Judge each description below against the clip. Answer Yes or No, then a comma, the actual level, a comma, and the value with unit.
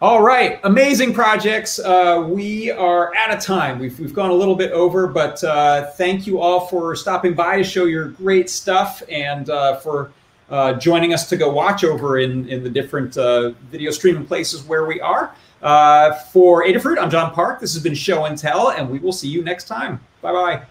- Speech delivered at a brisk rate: Yes, fast, 210 wpm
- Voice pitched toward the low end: No, medium, 170 Hz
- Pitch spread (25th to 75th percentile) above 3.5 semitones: Yes, average, 4.1 semitones